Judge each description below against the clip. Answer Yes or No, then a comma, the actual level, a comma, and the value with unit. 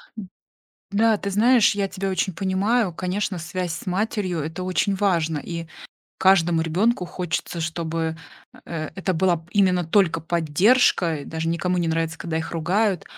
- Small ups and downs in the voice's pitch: No, average, 3.1 semitones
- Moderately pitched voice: Yes, medium, 180 Hz